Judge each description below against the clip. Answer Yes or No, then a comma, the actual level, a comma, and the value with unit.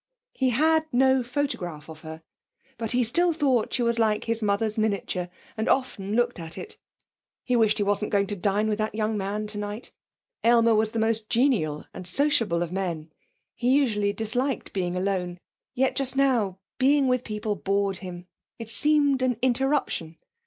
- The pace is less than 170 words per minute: No, average, 175 wpm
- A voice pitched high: Yes, high, 220 Hz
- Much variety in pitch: No, average, 4.3 semitones